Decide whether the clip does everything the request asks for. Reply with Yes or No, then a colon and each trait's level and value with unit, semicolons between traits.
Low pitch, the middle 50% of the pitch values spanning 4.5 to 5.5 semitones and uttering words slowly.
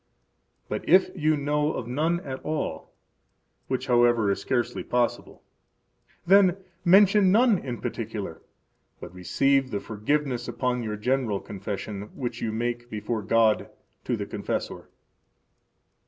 Yes: low, 120 Hz; average, 5.2 semitones; slow, 125 wpm